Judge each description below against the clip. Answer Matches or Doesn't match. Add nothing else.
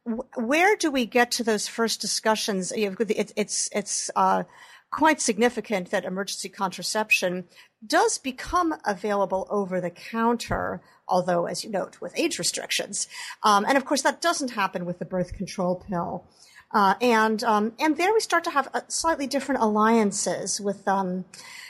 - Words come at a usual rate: Matches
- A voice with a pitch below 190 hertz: Doesn't match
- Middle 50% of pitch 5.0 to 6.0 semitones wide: Matches